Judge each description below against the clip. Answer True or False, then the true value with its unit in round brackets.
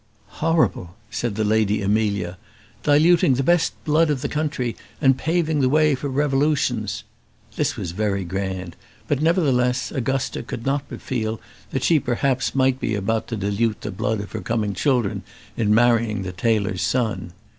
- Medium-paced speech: True (165 wpm)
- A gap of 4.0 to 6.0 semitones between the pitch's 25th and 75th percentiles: True (5.2 semitones)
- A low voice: True (120 Hz)